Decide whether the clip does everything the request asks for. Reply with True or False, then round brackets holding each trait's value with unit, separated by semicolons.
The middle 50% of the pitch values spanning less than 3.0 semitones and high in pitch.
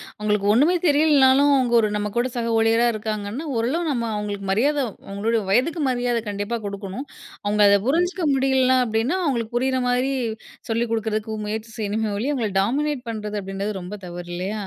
False (3.9 semitones; 230 Hz)